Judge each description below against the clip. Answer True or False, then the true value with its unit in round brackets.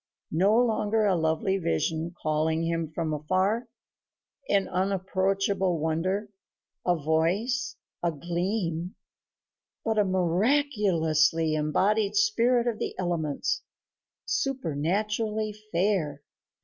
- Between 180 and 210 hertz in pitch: True (185 Hz)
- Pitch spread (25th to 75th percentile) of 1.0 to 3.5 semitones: False (4.8 semitones)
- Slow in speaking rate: True (95 wpm)